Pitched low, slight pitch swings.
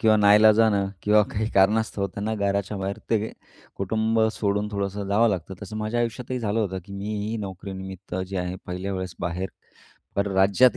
Yes: low, 100 Hz; narrow, 2.1 semitones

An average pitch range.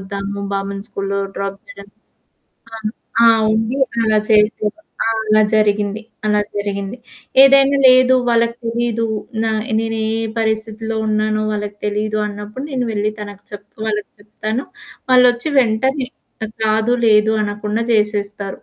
No: narrow, 1.9 semitones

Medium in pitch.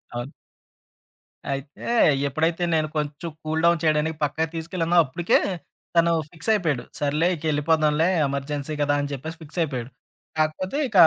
Yes: medium, 155 Hz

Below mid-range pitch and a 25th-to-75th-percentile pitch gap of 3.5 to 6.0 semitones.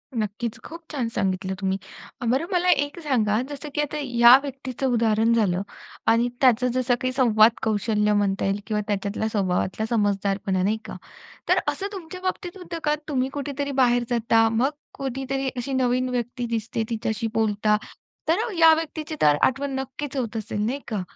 No: high, 240 Hz; average, 4.2 semitones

